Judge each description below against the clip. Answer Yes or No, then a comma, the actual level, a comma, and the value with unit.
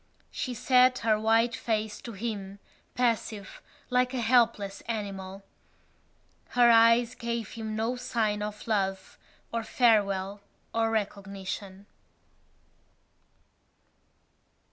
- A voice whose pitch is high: Yes, high, 220 Hz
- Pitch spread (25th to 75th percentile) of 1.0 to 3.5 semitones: Yes, average, 2.7 semitones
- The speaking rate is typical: No, slow, 100 wpm